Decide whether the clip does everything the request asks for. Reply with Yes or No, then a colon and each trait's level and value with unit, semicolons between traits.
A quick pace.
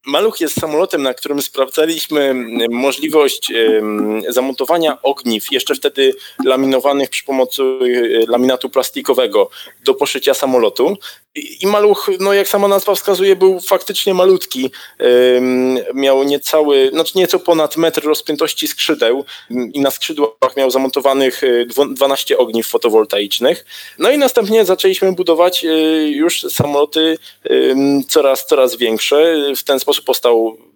No: average, 115 wpm